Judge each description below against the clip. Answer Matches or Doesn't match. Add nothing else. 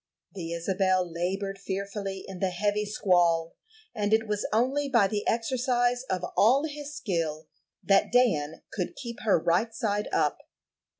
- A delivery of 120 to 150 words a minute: Matches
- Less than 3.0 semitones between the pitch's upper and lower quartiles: Doesn't match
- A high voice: Matches